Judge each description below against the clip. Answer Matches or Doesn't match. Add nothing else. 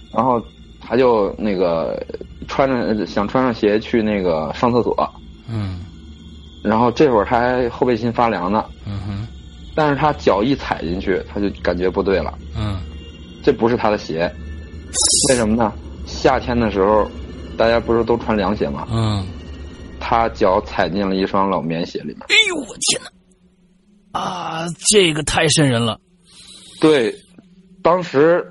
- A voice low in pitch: Matches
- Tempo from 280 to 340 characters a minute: Doesn't match